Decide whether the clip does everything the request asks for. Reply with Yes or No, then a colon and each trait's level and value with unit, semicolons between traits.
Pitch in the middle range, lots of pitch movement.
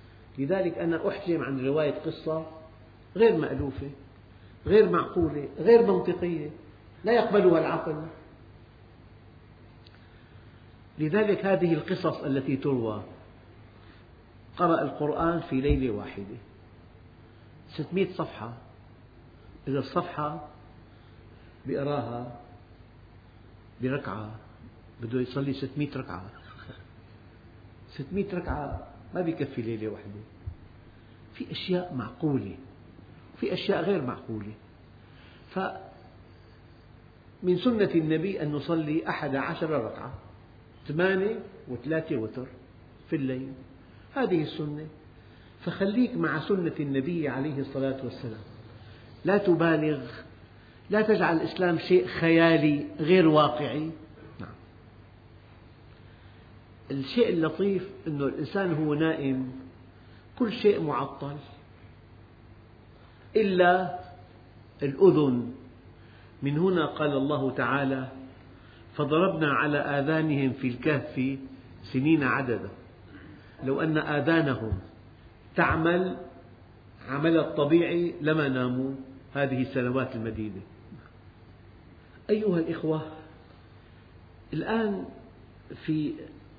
No: low, 130 Hz; wide, 6.4 semitones